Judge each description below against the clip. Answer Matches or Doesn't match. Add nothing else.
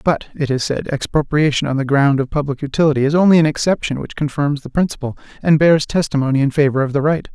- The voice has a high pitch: Doesn't match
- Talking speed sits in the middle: Doesn't match